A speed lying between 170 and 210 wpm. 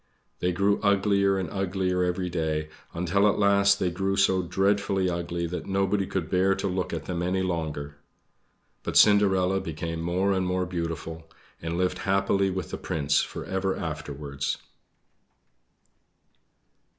No: average, 145 wpm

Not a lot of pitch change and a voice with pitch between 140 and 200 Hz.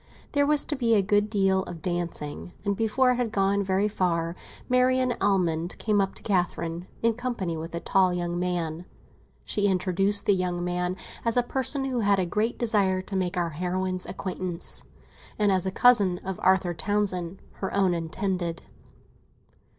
No: average, 3.0 semitones; high, 190 Hz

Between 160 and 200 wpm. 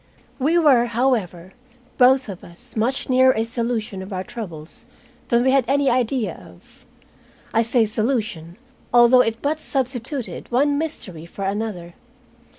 No: average, 145 wpm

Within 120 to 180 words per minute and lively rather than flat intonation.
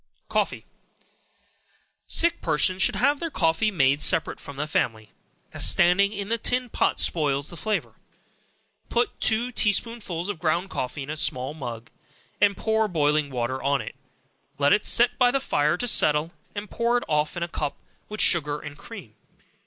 Yes: average, 175 wpm; wide, 6.9 semitones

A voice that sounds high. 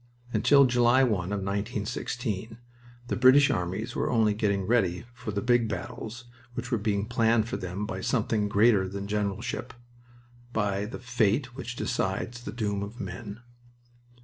No: low, 110 Hz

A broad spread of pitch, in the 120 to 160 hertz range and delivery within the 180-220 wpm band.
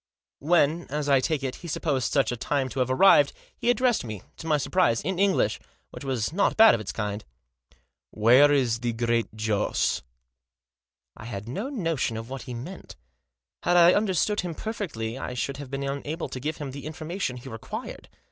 Yes: wide, 6.2 semitones; medium, 140 Hz; average, 195 wpm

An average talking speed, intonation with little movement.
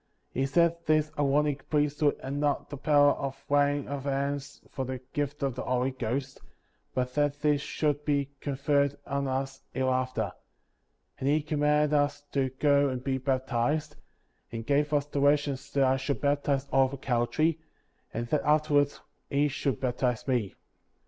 Yes: average, 160 wpm; narrow, 1.7 semitones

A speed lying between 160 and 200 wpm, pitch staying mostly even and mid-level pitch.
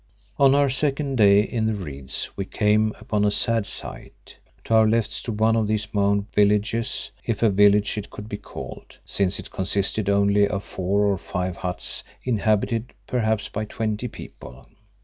No: average, 170 wpm; narrow, 2.0 semitones; low, 105 Hz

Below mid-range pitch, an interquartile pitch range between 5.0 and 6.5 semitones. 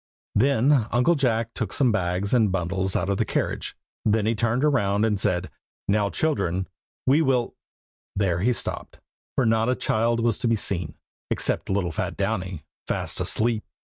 No: low, 110 Hz; average, 3.9 semitones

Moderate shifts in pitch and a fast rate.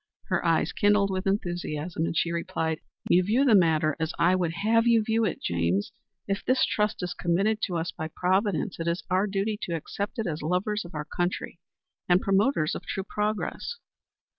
No: average, 3.8 semitones; average, 190 wpm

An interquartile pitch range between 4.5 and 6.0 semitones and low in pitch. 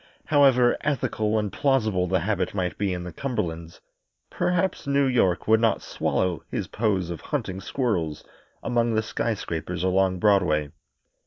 Yes: average, 5.1 semitones; low, 100 Hz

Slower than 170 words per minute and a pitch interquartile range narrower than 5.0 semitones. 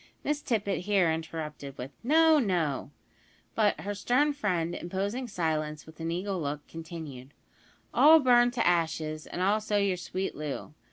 No: average, 150 wpm; average, 5.3 semitones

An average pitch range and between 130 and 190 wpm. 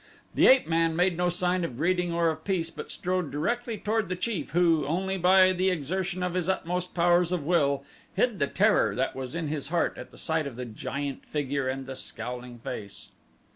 No: average, 4.3 semitones; fast, 205 wpm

